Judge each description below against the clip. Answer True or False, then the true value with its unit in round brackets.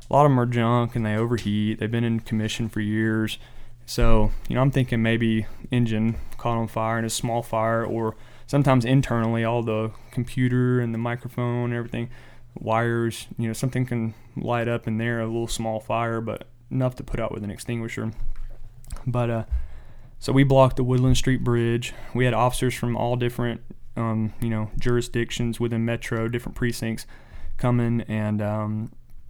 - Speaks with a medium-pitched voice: False (115 Hz)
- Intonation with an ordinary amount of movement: False (1.4 semitones)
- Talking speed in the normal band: True (180 wpm)